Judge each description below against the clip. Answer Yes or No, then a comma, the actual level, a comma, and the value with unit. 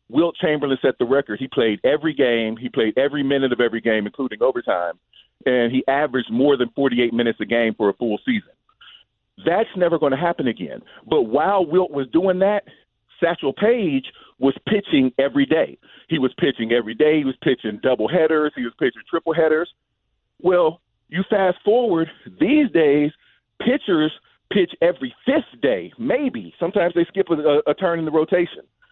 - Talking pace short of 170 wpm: No, average, 175 wpm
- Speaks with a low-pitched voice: No, medium, 155 Hz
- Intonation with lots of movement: Yes, wide, 6.1 semitones